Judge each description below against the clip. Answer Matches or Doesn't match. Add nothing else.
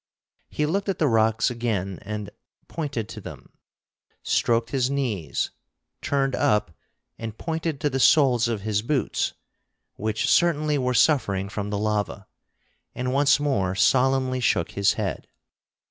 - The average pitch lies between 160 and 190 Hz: Doesn't match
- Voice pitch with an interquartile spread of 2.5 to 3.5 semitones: Doesn't match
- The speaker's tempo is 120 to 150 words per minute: Matches